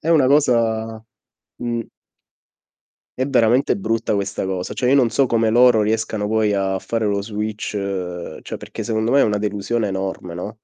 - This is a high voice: No, low, 110 Hz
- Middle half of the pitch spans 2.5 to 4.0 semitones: Yes, average, 2.8 semitones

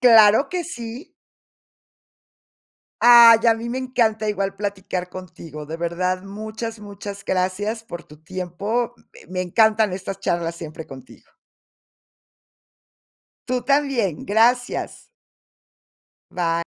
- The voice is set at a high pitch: Yes, high, 205 Hz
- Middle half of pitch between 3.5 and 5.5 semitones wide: Yes, average, 4.1 semitones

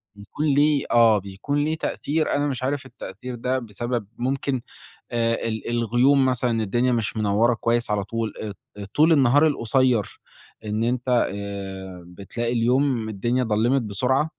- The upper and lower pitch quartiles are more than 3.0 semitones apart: Yes, average, 3.5 semitones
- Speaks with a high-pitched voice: No, low, 120 Hz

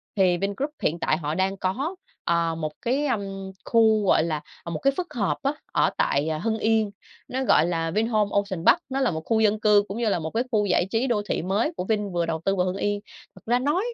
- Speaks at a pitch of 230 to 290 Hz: No, high, 205 Hz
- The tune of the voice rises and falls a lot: No, average, 4.7 semitones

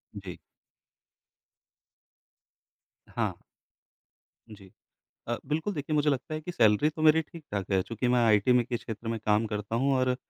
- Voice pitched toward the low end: Yes, low, 120 Hz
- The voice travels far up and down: Yes, wide, 5.9 semitones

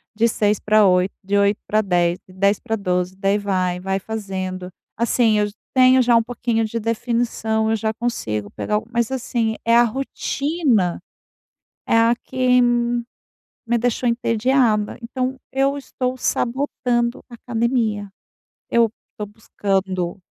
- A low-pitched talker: No, high, 225 Hz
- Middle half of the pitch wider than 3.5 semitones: No, average, 3.2 semitones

